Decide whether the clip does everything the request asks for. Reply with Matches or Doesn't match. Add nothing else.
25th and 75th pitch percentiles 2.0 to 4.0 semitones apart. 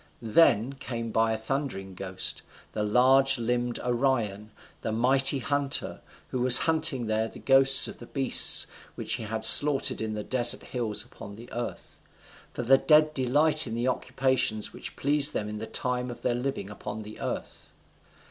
Matches